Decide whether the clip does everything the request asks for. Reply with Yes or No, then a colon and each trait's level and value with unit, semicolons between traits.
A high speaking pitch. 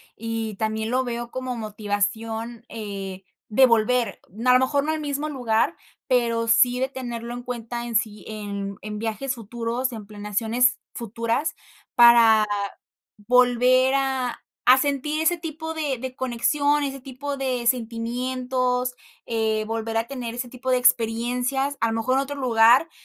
Yes: high, 240 Hz